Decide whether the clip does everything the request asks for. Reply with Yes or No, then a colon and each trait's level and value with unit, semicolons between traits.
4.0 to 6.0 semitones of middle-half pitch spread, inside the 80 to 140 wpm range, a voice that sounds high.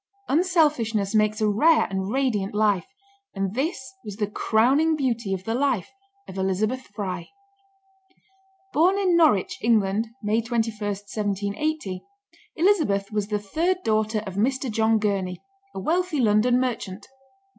Yes: average, 5.0 semitones; slow, 135 wpm; high, 220 Hz